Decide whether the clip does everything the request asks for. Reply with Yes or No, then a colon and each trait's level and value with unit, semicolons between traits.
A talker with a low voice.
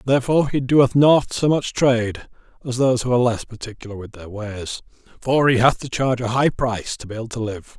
Yes: low, 120 Hz